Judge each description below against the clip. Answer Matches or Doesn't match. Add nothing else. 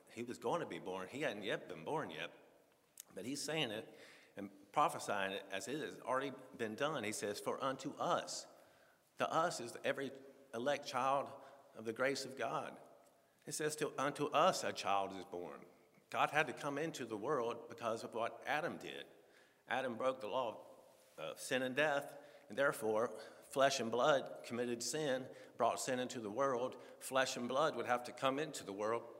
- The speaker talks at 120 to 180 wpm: Doesn't match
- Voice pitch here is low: Matches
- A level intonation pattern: Doesn't match